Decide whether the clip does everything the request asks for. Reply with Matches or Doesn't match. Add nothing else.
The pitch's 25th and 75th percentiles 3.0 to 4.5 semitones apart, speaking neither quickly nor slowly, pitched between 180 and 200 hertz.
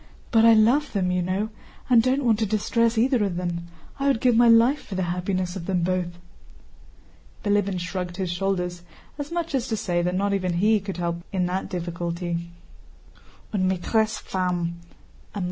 Matches